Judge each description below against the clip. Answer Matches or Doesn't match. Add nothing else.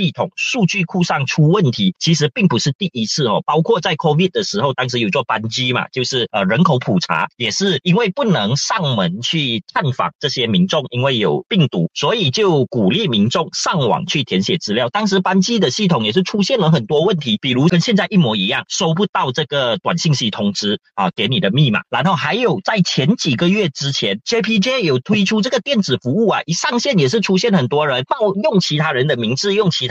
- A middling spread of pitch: Doesn't match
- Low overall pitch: Doesn't match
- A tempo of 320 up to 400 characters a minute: Matches